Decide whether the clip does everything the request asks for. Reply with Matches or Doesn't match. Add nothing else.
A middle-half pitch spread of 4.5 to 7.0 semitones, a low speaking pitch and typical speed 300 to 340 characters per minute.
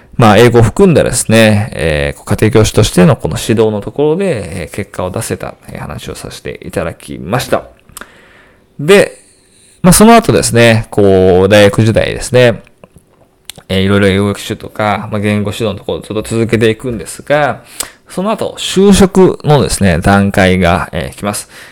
Doesn't match